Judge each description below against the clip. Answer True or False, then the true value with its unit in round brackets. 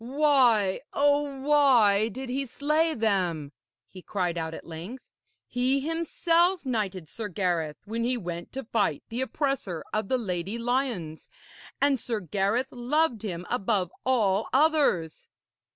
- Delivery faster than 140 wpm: False (135 wpm)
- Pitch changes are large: True (6.3 semitones)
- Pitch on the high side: True (230 Hz)